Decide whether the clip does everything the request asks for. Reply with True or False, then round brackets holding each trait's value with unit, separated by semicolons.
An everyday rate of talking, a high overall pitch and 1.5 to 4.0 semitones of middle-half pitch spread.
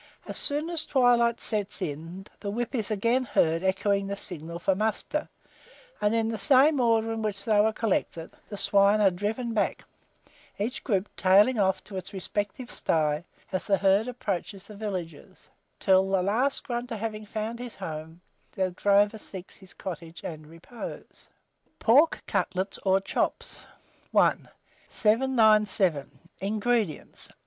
True (145 wpm; 205 Hz; 3.3 semitones)